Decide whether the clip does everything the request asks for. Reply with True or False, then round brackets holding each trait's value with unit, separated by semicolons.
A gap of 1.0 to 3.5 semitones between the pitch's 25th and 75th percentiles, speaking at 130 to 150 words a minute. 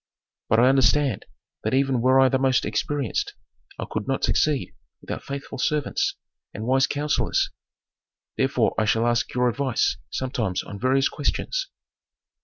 True (2.6 semitones; 145 wpm)